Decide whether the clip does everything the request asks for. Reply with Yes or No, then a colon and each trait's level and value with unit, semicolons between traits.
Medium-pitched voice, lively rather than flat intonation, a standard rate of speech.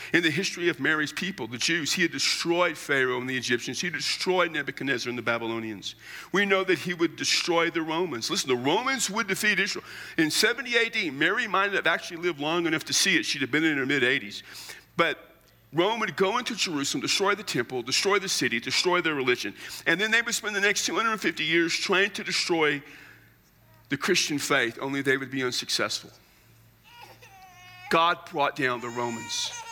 Yes: medium, 165 Hz; wide, 6.3 semitones; average, 190 wpm